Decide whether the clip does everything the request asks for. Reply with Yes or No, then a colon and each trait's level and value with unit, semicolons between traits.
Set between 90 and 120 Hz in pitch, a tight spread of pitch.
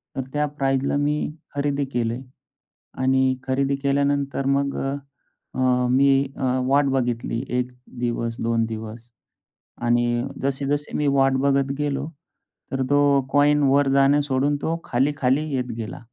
No: low, 135 Hz; narrow, 2.1 semitones